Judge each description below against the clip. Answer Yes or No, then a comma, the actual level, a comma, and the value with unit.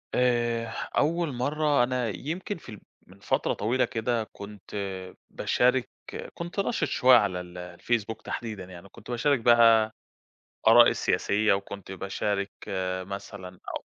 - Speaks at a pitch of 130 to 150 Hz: No, low, 115 Hz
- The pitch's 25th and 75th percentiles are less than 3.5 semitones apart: No, average, 4.3 semitones